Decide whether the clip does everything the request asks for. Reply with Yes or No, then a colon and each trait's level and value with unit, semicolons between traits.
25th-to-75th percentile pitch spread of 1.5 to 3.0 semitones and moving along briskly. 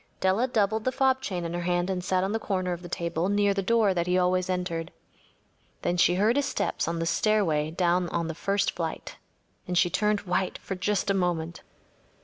Yes: narrow, 2.6 semitones; fast, 220 wpm